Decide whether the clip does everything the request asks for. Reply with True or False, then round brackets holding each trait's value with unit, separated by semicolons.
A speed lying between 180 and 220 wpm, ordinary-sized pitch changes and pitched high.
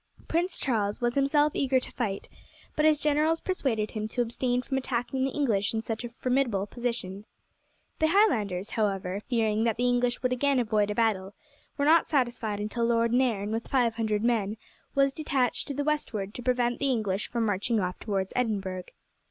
True (185 wpm; 4.1 semitones; 235 Hz)